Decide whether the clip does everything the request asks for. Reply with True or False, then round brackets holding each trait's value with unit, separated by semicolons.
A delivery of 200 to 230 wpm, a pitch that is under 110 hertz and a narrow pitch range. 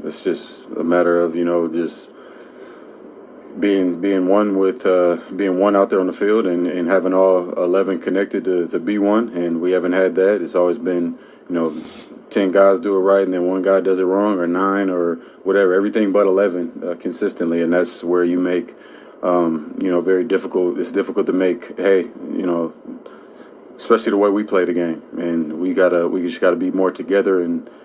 True (205 wpm; 90 Hz; 2.0 semitones)